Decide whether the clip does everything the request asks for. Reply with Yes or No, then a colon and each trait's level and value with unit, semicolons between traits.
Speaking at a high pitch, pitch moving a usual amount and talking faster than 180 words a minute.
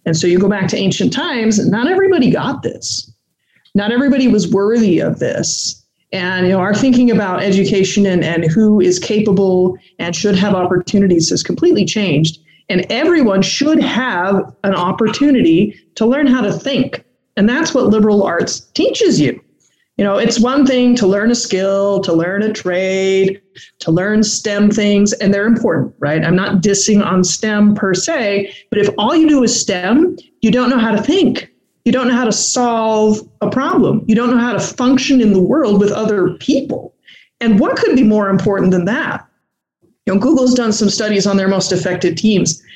Yes: high, 210 Hz; average, 3.9 semitones; average, 190 wpm